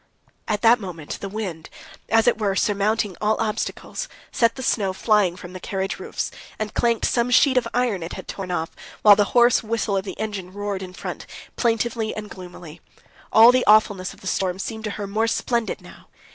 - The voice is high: Yes, high, 210 Hz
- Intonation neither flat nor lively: Yes, average, 3.0 semitones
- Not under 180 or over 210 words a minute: Yes, average, 200 wpm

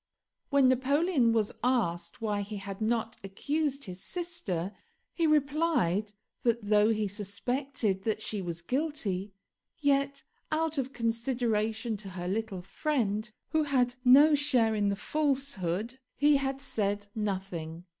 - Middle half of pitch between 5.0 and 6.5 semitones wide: Yes, wide, 5.6 semitones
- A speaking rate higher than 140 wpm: No, slow, 135 wpm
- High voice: Yes, high, 225 Hz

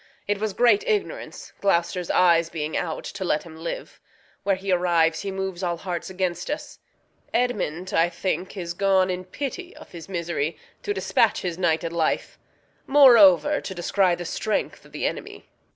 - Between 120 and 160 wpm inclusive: No, average, 170 wpm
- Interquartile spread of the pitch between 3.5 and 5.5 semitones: No, average, 2.7 semitones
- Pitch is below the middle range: No, medium, 180 Hz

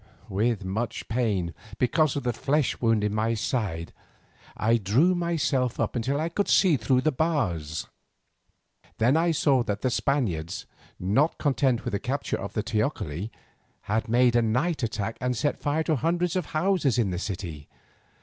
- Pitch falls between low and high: No, low, 120 Hz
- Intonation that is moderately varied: No, wide, 5.7 semitones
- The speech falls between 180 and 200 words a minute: No, average, 170 wpm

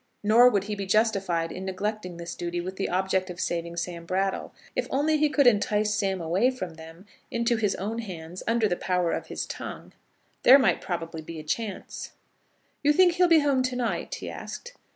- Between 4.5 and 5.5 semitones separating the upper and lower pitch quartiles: Yes, average, 5.1 semitones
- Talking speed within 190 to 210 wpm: Yes, average, 200 wpm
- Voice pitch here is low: No, high, 195 Hz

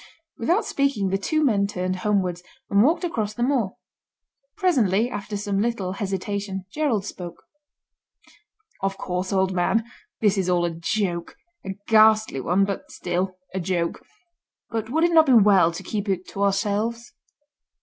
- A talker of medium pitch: No, high, 200 Hz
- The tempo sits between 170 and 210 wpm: No, average, 155 wpm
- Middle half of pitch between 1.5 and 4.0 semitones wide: Yes, average, 3.4 semitones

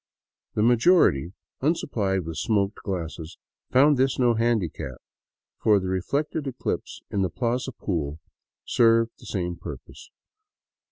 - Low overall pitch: Yes, low, 110 Hz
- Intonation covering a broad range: Yes, wide, 5.9 semitones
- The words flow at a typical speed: No, slow, 120 wpm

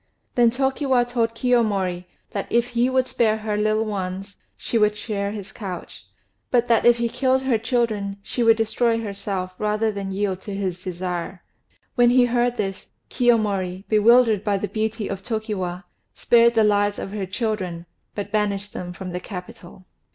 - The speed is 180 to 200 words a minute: No, average, 170 wpm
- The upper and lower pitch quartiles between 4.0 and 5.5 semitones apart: No, average, 3.3 semitones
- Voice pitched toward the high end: Yes, high, 210 Hz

